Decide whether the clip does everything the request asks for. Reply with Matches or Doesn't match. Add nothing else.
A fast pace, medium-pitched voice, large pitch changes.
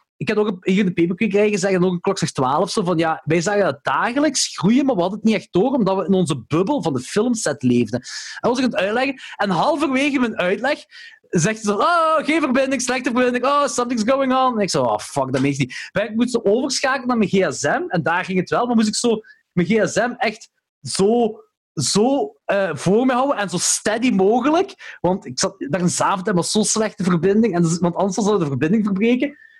Doesn't match